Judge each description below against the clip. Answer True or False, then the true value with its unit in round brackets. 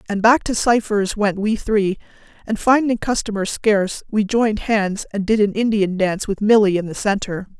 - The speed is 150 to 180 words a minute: False (190 wpm)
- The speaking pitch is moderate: False (210 Hz)